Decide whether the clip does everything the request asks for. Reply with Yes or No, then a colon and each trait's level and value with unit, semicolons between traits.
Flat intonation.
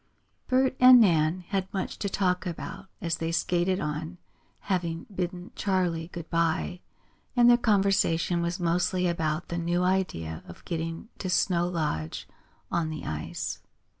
Yes: narrow, 2.3 semitones